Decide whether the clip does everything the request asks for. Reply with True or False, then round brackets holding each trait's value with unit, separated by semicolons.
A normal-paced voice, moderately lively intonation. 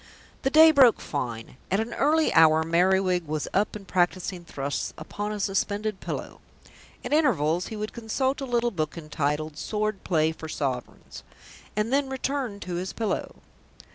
False (160 wpm; 6.6 semitones)